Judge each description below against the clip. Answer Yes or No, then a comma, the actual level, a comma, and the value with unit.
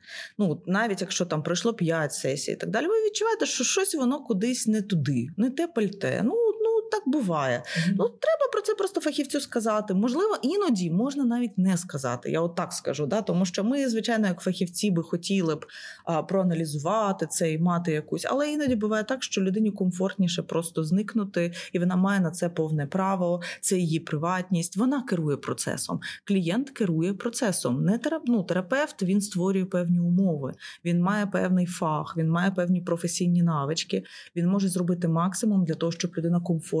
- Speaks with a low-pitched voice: No, high, 190 Hz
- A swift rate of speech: Yes, fast, 175 wpm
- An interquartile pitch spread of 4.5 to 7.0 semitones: Yes, average, 5.0 semitones